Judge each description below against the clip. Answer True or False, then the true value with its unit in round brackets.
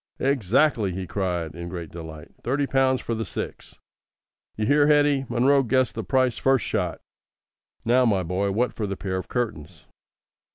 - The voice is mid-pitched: False (115 Hz)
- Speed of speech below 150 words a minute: False (165 wpm)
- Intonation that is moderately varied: False (6.2 semitones)